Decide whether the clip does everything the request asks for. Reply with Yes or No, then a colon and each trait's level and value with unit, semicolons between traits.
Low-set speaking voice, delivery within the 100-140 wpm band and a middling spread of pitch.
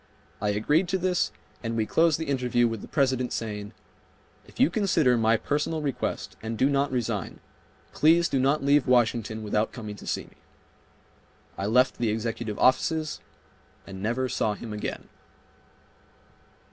No: low, 125 Hz; average, 155 wpm; average, 4.8 semitones